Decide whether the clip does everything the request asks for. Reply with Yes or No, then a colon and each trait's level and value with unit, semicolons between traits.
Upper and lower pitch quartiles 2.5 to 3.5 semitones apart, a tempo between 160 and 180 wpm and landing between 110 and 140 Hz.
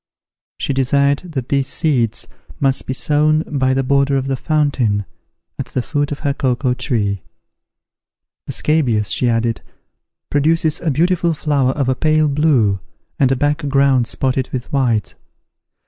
No: average, 2.8 semitones; average, 150 wpm; low, 135 Hz